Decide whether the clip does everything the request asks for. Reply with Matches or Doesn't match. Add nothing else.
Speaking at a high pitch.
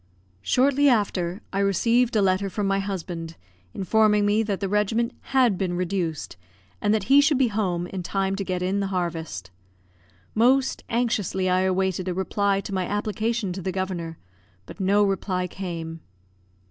Matches